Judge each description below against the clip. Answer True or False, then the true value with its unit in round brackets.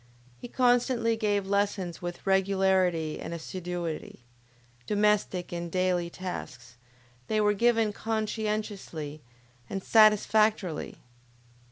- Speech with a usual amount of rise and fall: True (3.5 semitones)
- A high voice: True (195 Hz)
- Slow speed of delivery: True (90 wpm)